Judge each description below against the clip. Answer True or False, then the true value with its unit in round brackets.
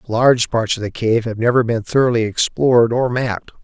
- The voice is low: True (115 Hz)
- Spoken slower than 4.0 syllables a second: False (5.6 syllables/s)